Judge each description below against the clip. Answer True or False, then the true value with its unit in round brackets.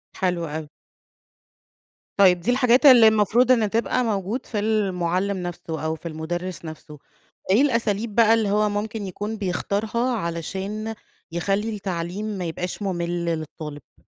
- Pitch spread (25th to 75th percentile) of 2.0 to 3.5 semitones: False (4.2 semitones)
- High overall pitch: True (200 Hz)